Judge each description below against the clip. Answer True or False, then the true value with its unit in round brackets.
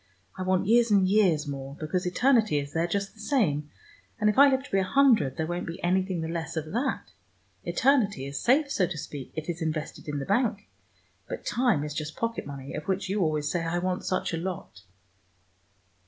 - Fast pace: True (215 wpm)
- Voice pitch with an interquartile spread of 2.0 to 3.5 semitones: False (5.4 semitones)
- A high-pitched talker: False (180 Hz)